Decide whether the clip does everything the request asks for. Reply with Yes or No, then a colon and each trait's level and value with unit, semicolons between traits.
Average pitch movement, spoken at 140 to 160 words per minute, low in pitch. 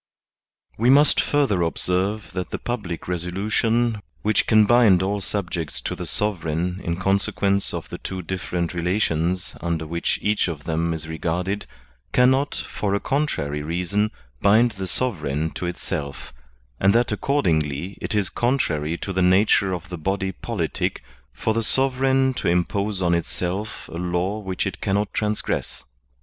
Yes: average, 3.7 semitones; average, 155 wpm; very low, 95 Hz